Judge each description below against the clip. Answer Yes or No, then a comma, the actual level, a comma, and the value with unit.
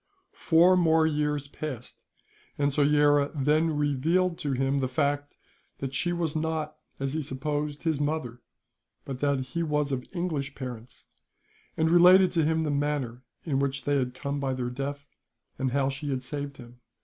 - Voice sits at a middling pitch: Yes, medium, 145 Hz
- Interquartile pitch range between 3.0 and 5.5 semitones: No, narrow, 2.6 semitones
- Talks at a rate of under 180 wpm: Yes, average, 170 wpm